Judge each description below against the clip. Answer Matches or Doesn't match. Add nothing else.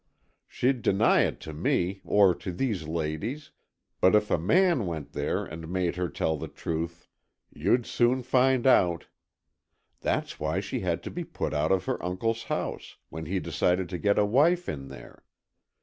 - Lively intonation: Matches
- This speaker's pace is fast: Doesn't match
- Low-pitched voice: Matches